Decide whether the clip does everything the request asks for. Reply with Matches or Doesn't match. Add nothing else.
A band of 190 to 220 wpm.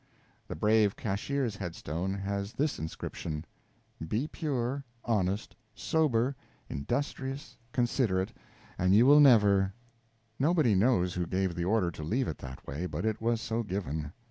Doesn't match